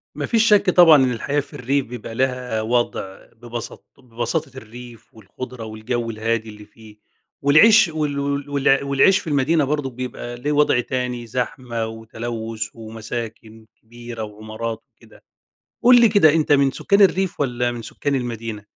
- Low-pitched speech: Yes, low, 125 Hz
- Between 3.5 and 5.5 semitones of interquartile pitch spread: Yes, average, 4.0 semitones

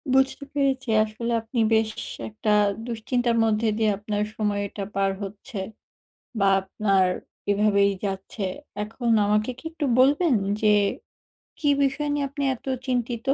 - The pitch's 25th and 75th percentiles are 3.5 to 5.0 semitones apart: Yes, average, 4.0 semitones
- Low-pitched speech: No, high, 220 Hz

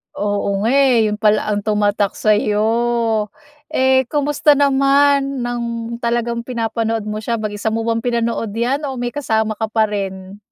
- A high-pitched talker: Yes, high, 230 Hz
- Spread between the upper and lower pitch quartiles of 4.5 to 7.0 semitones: No, average, 2.7 semitones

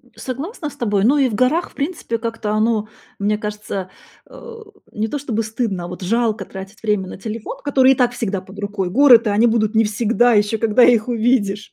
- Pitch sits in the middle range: No, high, 225 Hz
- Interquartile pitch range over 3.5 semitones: No, average, 3.0 semitones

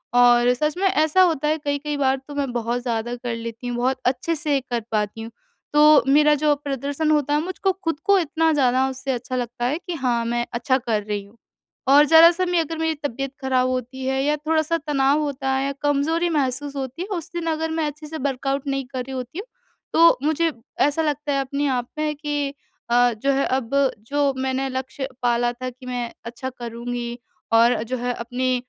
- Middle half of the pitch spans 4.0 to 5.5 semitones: No, average, 3.5 semitones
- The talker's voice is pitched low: No, very high, 270 Hz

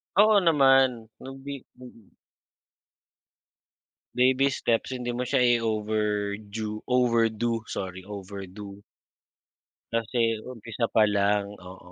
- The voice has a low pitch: Yes, low, 115 Hz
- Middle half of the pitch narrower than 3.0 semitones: No, average, 3.4 semitones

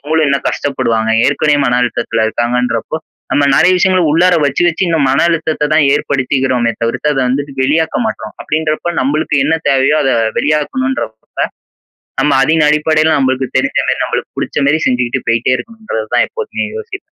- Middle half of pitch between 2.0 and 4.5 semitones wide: Yes, average, 3.7 semitones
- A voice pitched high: No, medium, 145 Hz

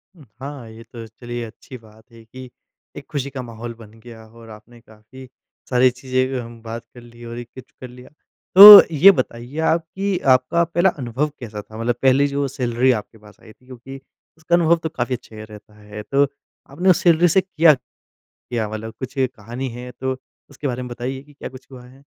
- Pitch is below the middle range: Yes, low, 125 Hz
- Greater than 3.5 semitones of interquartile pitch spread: No, average, 3.2 semitones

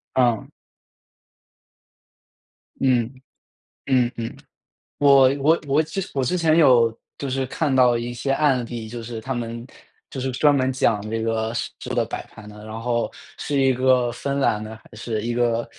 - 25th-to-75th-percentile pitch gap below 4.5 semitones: Yes, average, 2.8 semitones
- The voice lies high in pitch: No, low, 120 Hz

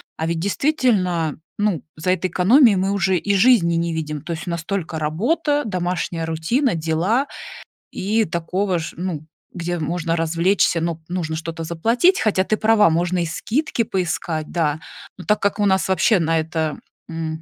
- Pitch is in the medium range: Yes, medium, 175 Hz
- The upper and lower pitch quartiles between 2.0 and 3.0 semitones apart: No, average, 3.7 semitones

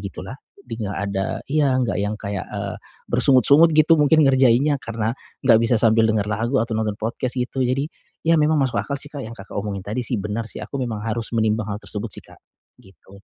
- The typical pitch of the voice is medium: No, low, 115 Hz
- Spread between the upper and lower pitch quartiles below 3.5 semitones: No, average, 4.1 semitones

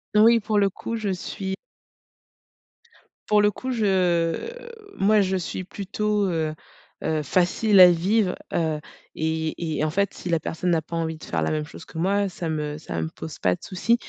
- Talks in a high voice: No, medium, 180 Hz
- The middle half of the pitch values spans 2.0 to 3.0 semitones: No, average, 4.2 semitones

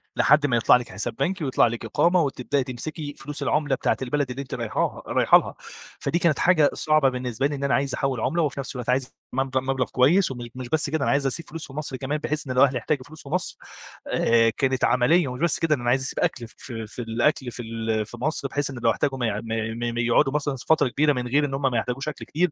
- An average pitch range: Yes, average, 3.3 semitones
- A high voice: No, low, 135 Hz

